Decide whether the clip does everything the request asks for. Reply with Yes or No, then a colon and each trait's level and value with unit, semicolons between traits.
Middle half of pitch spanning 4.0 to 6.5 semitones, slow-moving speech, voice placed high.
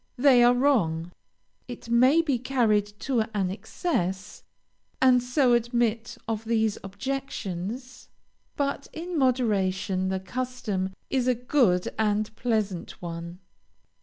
Yes: average, 4.8 semitones; slow, 115 wpm; high, 230 Hz